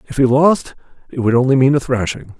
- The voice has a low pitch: Yes, low, 130 Hz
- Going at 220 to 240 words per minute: Yes, fast, 225 wpm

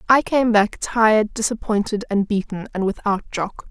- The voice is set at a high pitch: Yes, high, 215 Hz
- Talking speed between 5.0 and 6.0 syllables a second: No, 4.8 syllables/s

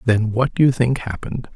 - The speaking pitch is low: Yes, low, 120 Hz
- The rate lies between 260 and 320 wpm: No, fast, 230 wpm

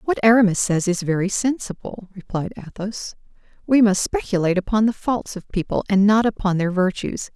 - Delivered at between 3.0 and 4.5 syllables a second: No, 5.4 syllables/s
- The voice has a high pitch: Yes, high, 200 Hz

